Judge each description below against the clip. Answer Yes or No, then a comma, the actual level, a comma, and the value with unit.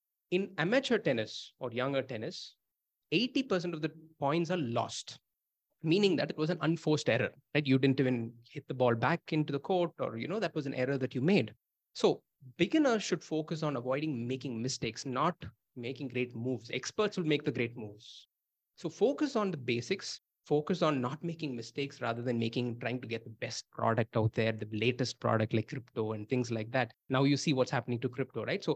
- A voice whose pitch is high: No, low, 135 Hz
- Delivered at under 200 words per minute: No, fast, 205 wpm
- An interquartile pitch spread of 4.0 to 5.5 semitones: Yes, average, 5.0 semitones